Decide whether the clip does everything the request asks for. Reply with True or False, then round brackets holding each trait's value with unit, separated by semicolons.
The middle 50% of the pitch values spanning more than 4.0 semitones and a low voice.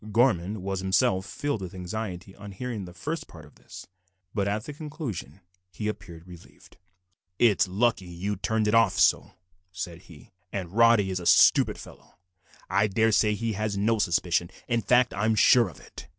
False (3.7 semitones; 100 Hz)